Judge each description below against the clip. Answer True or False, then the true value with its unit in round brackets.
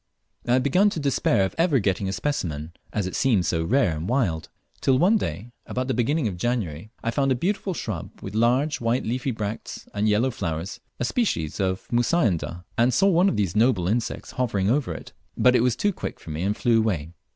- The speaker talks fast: True (215 wpm)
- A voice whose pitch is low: True (115 Hz)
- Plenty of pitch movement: True (5.7 semitones)